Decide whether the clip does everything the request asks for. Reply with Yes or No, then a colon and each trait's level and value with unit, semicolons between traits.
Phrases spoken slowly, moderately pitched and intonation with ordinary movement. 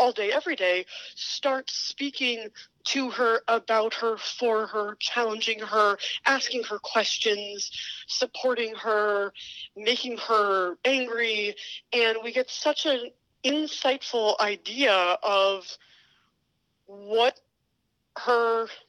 No: slow, 100 wpm; high, 230 Hz; average, 3.2 semitones